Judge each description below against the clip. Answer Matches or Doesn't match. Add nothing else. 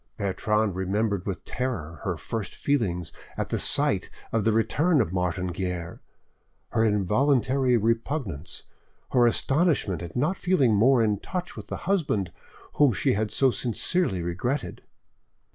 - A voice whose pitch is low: Matches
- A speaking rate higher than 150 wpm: Doesn't match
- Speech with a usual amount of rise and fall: Doesn't match